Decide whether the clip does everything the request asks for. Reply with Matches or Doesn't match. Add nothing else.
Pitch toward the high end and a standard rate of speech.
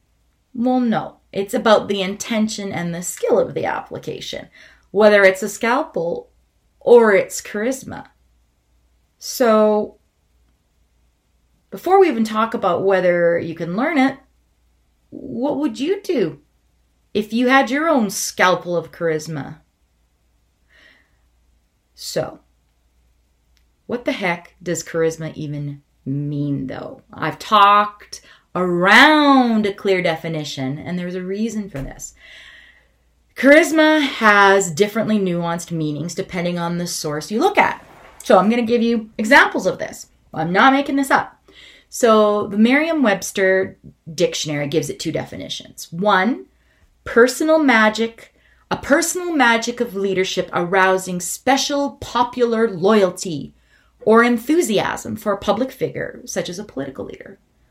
Doesn't match